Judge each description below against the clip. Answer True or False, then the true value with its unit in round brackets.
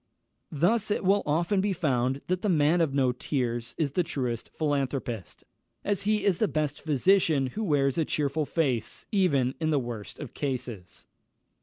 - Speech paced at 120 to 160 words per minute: False (170 wpm)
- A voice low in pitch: False (150 Hz)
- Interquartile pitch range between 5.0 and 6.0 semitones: True (5.5 semitones)